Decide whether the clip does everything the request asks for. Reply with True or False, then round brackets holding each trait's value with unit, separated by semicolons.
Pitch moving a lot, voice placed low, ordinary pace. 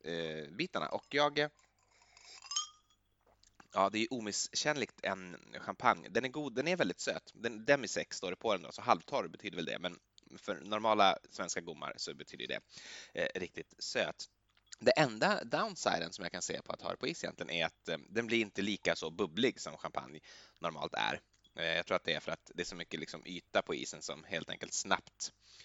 False (8.7 semitones; 110 Hz; 205 wpm)